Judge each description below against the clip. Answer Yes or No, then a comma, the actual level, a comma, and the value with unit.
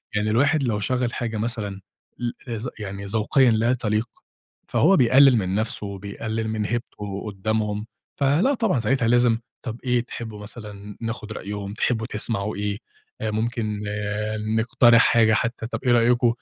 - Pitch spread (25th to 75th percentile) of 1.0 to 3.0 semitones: Yes, narrow, 2.6 semitones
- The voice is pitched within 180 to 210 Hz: No, low, 110 Hz